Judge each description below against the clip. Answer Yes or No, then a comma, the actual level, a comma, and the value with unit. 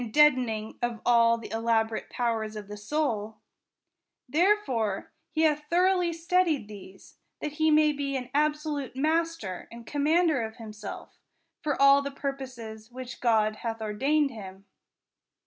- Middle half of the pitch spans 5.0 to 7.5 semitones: Yes, wide, 5.5 semitones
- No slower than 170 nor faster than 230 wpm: No, slow, 135 wpm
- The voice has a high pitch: Yes, very high, 255 Hz